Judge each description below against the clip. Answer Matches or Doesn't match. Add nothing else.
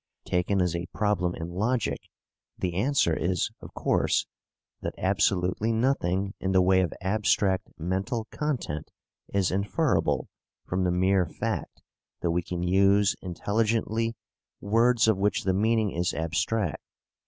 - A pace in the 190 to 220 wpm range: Doesn't match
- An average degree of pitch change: Matches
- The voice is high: Doesn't match